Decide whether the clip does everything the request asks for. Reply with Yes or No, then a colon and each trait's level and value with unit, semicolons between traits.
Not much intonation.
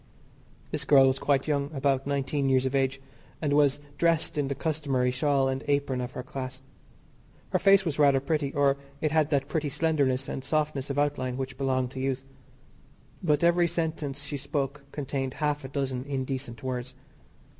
Yes: narrow, 1.9 semitones